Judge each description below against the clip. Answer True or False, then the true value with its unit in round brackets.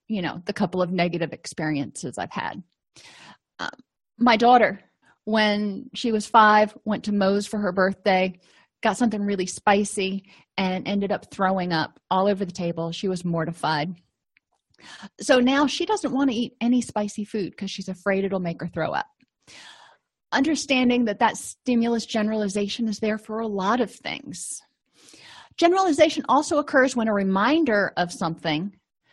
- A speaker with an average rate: True (155 wpm)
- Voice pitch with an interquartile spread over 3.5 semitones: True (4.1 semitones)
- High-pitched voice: True (205 Hz)